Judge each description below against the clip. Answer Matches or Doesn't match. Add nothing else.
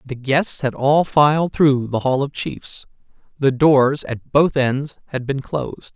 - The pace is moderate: Matches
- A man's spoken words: Matches